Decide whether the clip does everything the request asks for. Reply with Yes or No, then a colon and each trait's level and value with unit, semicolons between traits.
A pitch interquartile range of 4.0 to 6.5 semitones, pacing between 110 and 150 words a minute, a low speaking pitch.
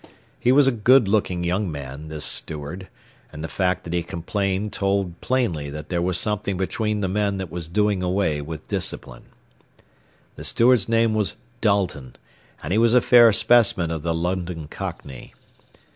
No: average, 4.4 semitones; average, 170 wpm; very low, 95 Hz